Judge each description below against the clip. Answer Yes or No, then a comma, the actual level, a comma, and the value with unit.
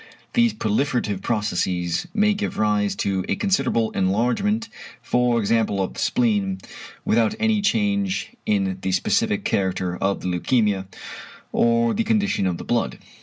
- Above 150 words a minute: No, average, 140 wpm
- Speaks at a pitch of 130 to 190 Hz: No, low, 115 Hz